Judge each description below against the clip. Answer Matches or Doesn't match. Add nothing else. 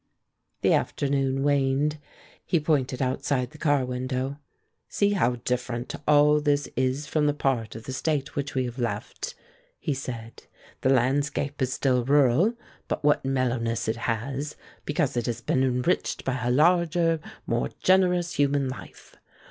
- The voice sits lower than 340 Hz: Matches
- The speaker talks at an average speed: Matches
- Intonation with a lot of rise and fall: Doesn't match